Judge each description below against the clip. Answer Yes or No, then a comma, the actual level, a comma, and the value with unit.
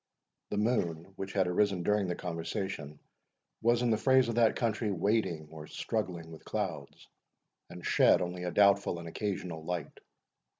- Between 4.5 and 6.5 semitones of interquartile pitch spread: No, average, 3.9 semitones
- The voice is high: No, very low, 95 Hz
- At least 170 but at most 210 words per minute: No, average, 160 wpm